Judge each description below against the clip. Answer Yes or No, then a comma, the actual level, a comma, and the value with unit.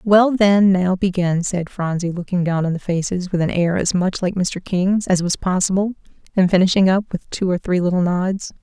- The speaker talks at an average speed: No, fast, 215 wpm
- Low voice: No, medium, 185 Hz